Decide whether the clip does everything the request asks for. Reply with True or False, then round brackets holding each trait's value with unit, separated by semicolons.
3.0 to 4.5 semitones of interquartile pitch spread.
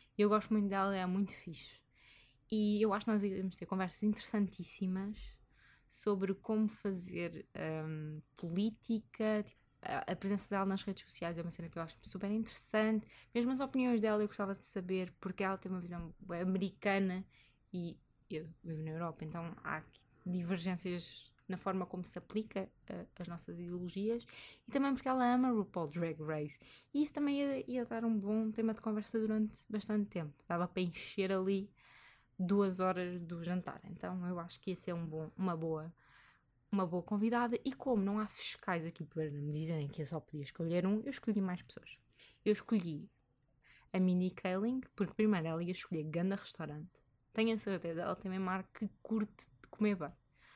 True (3.8 semitones)